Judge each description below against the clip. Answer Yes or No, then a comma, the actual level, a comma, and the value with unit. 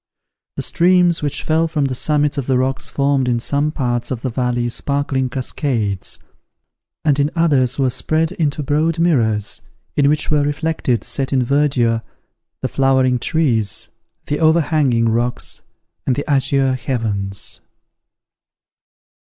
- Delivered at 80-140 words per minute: Yes, slow, 135 wpm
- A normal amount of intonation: Yes, average, 3.4 semitones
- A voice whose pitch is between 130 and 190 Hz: Yes, low, 135 Hz